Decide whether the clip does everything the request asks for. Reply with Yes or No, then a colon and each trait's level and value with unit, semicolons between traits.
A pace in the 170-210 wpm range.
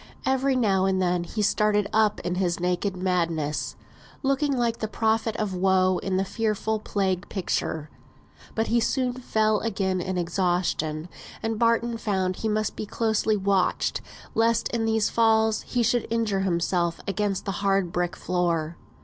No: average, 160 wpm